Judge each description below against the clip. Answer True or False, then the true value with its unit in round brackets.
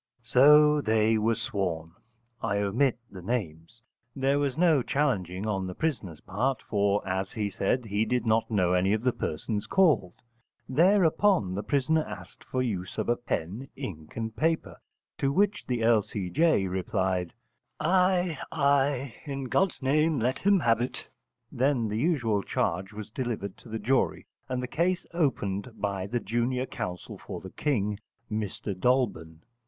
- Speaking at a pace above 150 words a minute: True (160 wpm)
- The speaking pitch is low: True (115 Hz)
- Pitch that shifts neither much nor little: False (6.0 semitones)